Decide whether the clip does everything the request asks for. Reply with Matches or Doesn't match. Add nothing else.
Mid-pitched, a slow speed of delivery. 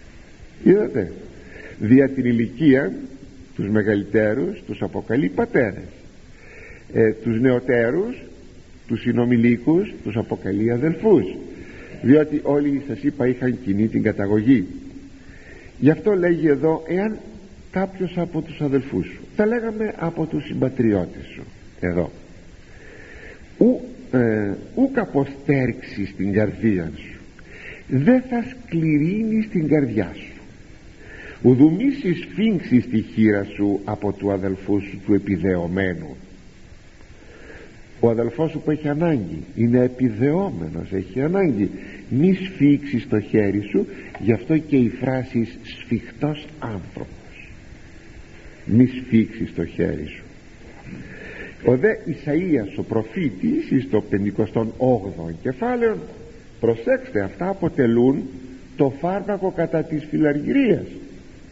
Doesn't match